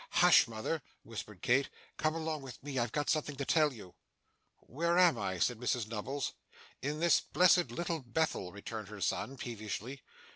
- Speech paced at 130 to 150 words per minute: No, average, 170 wpm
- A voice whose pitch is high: No, low, 135 Hz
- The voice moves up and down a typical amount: No, wide, 5.8 semitones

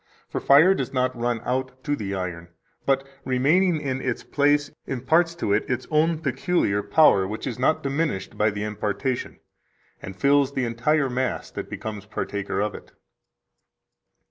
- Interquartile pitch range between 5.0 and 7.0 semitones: Yes, average, 5.3 semitones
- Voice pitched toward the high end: No, low, 130 Hz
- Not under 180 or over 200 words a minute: No, average, 160 wpm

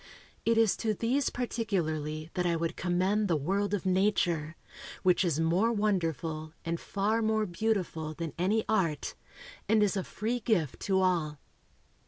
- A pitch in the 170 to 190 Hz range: Yes, medium, 185 Hz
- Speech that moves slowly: No, average, 155 wpm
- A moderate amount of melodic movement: Yes, average, 4.6 semitones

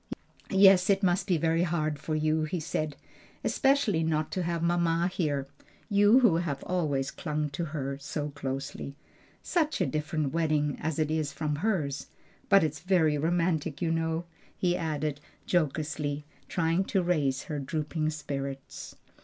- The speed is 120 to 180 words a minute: Yes, average, 155 wpm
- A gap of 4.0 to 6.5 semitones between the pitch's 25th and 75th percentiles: No, average, 2.9 semitones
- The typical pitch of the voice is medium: Yes, medium, 155 Hz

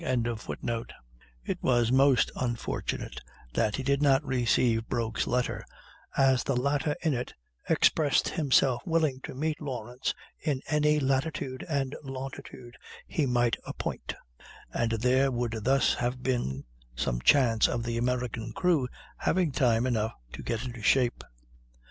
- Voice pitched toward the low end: Yes, low, 125 Hz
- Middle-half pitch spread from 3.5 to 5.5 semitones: No, average, 2.8 semitones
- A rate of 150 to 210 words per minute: No, slow, 135 wpm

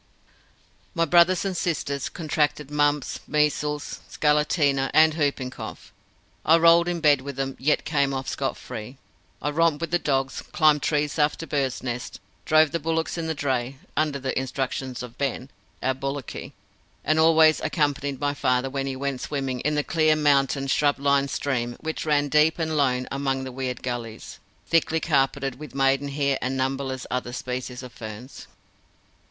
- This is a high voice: No, medium, 140 Hz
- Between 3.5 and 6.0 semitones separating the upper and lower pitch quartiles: No, narrow, 2.5 semitones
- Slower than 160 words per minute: No, average, 165 wpm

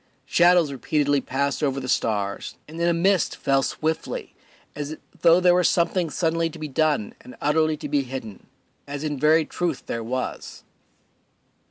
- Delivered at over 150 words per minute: Yes, average, 165 wpm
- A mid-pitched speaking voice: Yes, medium, 150 Hz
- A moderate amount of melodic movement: Yes, average, 3.5 semitones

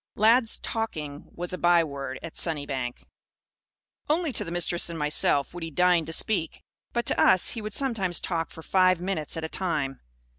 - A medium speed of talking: Yes, average, 180 wpm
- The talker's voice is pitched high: No, medium, 175 Hz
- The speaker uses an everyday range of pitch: Yes, average, 4.0 semitones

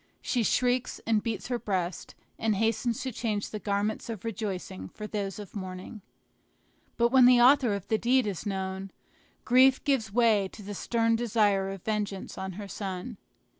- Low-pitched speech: No, high, 215 Hz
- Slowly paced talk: No, average, 170 wpm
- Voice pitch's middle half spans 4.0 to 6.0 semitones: No, average, 3.3 semitones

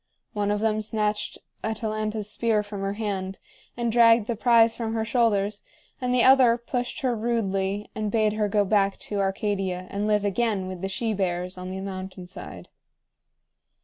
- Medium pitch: No, high, 210 Hz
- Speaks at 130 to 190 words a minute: Yes, average, 175 wpm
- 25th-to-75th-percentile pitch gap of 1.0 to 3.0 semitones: Yes, narrow, 2.5 semitones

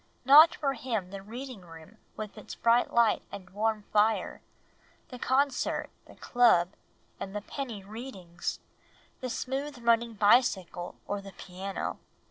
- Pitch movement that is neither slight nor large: Yes, average, 4.2 semitones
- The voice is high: Yes, high, 220 Hz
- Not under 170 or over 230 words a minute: No, slow, 135 wpm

